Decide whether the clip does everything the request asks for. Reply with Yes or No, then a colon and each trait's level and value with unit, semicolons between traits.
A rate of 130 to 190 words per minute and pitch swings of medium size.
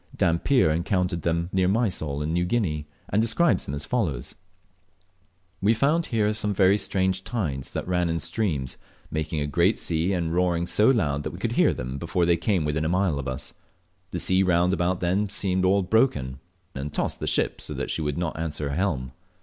No: average, 200 wpm; average, 4.3 semitones